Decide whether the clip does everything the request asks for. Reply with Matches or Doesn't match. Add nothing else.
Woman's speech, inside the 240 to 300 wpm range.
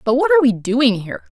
Matches